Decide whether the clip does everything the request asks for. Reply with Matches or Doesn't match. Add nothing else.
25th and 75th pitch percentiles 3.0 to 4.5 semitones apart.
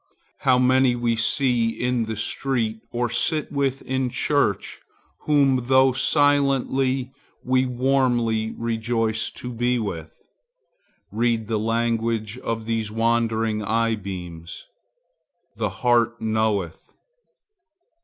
Doesn't match